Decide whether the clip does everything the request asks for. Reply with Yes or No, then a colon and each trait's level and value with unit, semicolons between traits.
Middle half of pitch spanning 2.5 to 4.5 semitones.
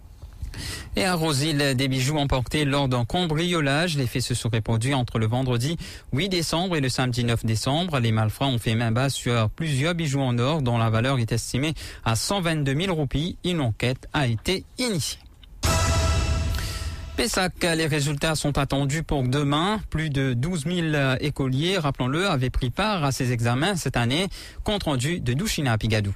No: average, 5.2 semitones